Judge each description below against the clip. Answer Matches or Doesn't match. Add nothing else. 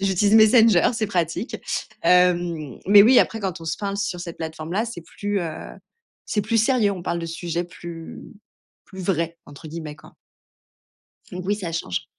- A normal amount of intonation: Matches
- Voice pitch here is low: Doesn't match